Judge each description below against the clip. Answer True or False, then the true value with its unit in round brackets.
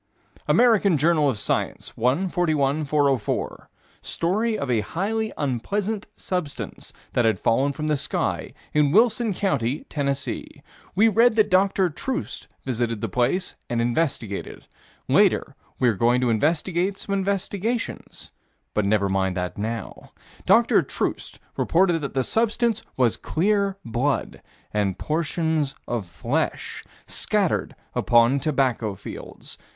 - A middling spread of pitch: False (8.3 semitones)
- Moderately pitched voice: True (150 Hz)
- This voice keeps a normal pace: False (125 wpm)